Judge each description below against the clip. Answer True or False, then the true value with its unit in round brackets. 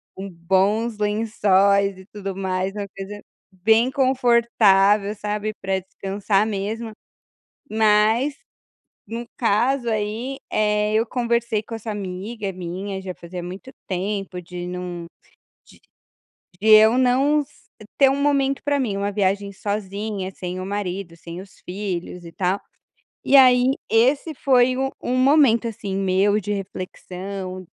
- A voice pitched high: True (205 Hz)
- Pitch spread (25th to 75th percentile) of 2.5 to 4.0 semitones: True (3.5 semitones)